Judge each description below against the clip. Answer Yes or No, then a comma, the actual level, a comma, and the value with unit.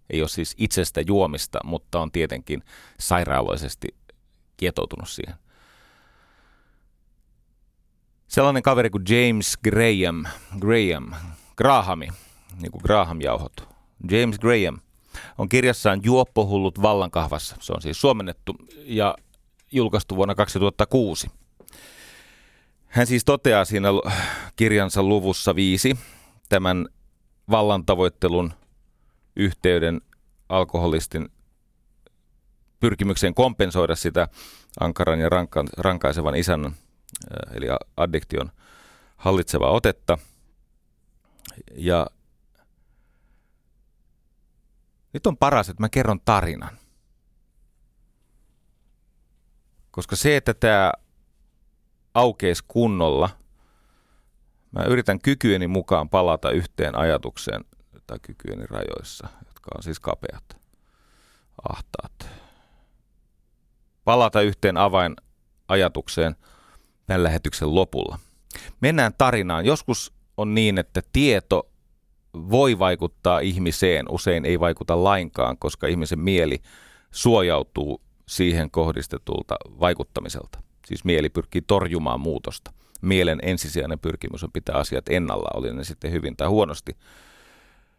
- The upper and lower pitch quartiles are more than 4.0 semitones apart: Yes, average, 4.5 semitones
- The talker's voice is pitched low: Yes, very low, 95 Hz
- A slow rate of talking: Yes, slow, 90 wpm